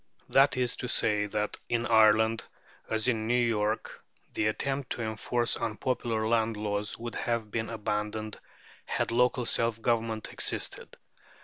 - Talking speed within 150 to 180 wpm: No, average, 140 wpm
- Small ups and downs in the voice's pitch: Yes, narrow, 1.7 semitones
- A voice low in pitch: Yes, low, 110 Hz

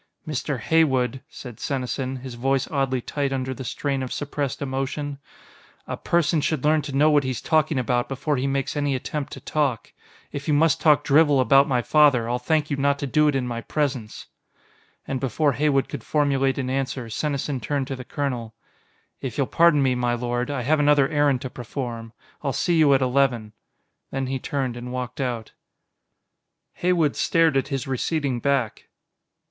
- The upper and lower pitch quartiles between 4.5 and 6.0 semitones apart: No, narrow, 2.5 semitones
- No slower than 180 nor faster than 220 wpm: Yes, average, 185 wpm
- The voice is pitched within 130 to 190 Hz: Yes, low, 135 Hz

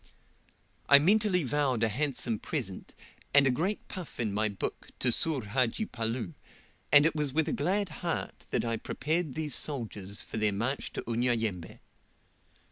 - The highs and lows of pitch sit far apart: Yes, wide, 5.7 semitones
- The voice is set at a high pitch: No, low, 130 Hz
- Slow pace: No, average, 160 wpm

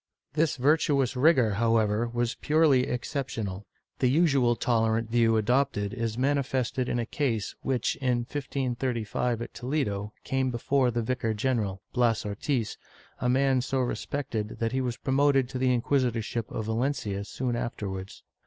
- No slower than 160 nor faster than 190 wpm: No, average, 145 wpm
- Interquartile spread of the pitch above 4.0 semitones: No, average, 2.9 semitones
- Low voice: Yes, low, 125 Hz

